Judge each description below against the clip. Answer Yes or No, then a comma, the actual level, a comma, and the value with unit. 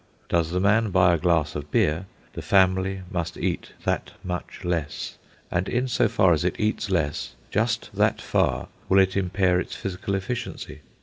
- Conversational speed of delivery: Yes, average, 175 wpm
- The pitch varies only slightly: Yes, narrow, 2.3 semitones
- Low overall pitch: Yes, very low, 95 Hz